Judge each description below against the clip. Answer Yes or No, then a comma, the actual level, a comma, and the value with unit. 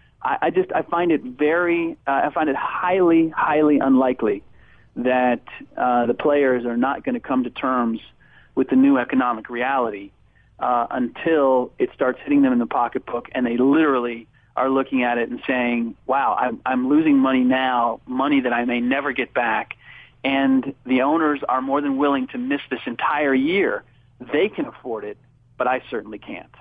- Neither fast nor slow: Yes, average, 180 wpm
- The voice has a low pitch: Yes, low, 130 Hz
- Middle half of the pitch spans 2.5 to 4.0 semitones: No, average, 4.8 semitones